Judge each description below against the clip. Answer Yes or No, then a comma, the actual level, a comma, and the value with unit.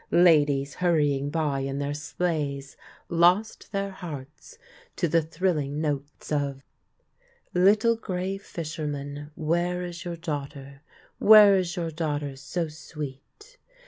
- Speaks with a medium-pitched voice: Yes, medium, 155 Hz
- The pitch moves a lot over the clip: No, average, 3.8 semitones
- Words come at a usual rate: No, slow, 120 wpm